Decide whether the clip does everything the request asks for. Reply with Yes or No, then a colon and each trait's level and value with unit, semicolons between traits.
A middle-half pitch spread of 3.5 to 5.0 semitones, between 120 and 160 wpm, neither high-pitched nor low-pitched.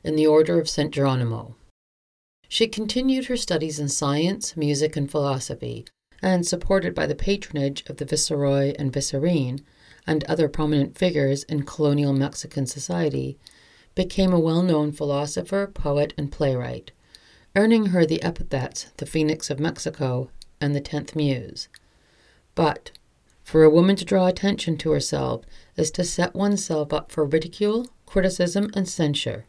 Yes: average, 4.1 semitones; average, 145 wpm; medium, 155 Hz